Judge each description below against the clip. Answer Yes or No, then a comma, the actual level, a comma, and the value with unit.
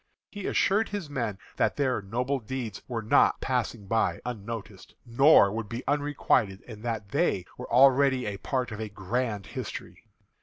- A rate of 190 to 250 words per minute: No, average, 160 wpm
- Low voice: Yes, low, 120 Hz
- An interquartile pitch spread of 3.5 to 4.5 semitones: Yes, average, 4.2 semitones